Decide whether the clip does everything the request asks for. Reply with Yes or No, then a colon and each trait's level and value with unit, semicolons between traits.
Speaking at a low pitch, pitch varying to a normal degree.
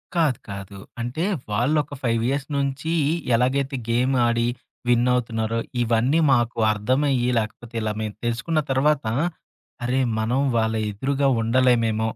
Yes: low, 120 Hz; average, 3.1 semitones